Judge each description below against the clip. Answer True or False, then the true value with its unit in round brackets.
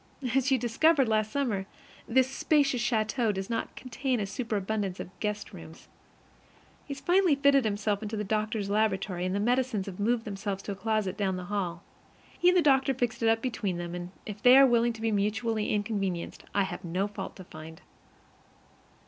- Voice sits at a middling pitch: False (215 Hz)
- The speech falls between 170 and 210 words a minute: True (190 wpm)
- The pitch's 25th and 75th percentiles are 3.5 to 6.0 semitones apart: True (4.0 semitones)